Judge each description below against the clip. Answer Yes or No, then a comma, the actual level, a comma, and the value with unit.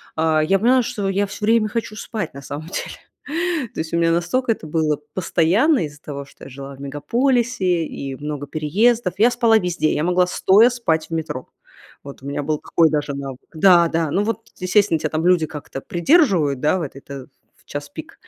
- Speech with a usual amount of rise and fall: No, wide, 6.2 semitones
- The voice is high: No, medium, 170 Hz